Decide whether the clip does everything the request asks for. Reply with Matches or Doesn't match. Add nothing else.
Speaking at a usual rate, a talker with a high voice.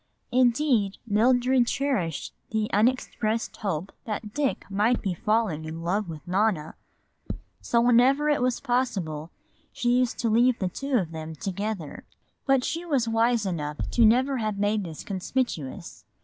Matches